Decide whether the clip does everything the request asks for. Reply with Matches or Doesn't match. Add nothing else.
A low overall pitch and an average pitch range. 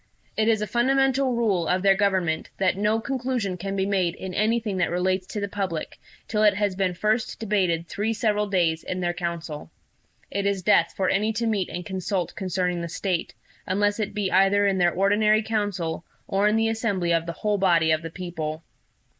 Doesn't match